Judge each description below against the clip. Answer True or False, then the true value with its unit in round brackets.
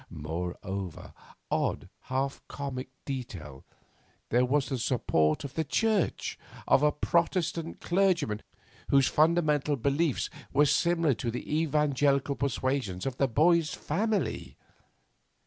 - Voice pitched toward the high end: False (140 Hz)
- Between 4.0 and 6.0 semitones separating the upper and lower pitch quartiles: True (4.6 semitones)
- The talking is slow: True (110 wpm)